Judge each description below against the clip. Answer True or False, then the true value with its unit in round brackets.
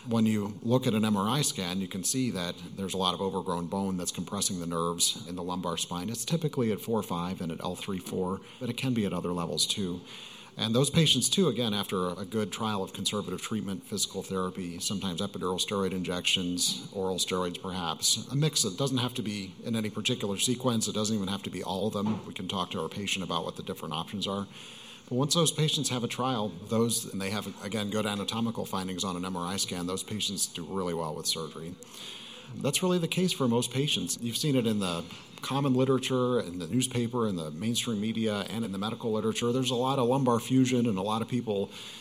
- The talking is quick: True (225 wpm)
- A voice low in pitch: True (110 Hz)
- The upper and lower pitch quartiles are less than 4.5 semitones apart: False (4.8 semitones)